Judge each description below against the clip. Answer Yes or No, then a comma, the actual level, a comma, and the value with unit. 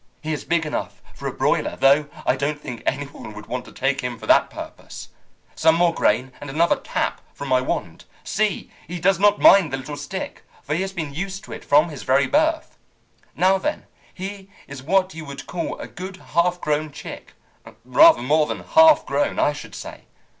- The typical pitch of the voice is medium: Yes, medium, 155 Hz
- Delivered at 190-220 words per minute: Yes, fast, 205 wpm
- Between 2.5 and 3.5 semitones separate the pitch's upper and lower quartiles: No, average, 5.3 semitones